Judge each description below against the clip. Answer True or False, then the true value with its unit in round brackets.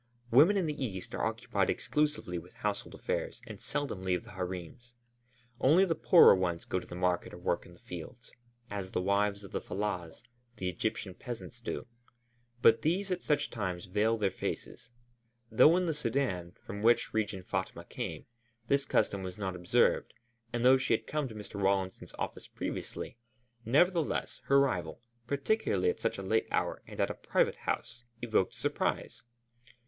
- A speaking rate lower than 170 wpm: False (175 wpm)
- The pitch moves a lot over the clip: True (7.0 semitones)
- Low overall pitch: True (105 Hz)